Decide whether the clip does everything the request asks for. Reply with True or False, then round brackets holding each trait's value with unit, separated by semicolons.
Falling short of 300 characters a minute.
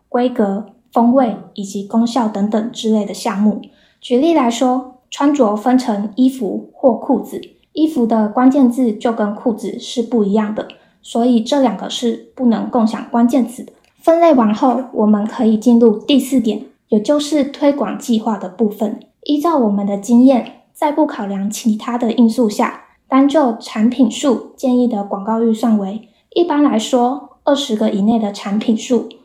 True (250 characters per minute)